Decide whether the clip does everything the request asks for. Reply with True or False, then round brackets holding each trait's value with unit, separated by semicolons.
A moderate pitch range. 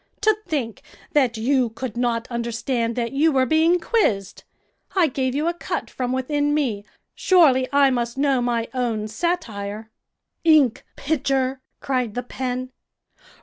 True (3.7 semitones)